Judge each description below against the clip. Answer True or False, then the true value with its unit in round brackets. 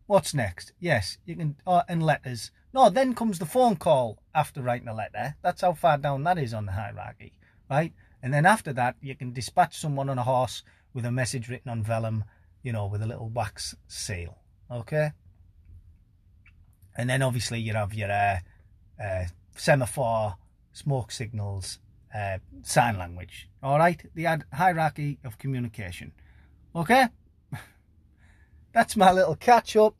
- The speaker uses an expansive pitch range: True (7.4 semitones)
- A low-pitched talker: True (115 Hz)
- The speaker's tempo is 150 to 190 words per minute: True (160 wpm)